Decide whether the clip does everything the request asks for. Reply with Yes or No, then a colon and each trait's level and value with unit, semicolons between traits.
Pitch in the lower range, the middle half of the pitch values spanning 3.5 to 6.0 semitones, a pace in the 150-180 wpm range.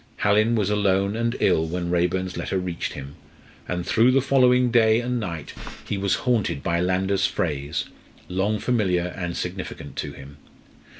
Yes: very low, 95 Hz; average, 4.2 semitones; average, 160 wpm